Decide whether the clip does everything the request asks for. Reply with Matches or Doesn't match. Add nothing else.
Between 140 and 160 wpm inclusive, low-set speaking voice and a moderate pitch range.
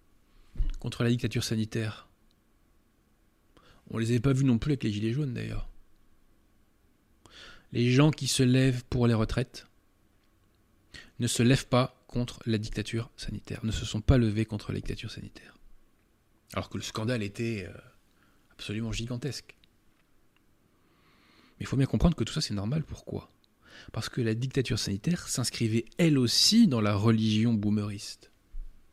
Matches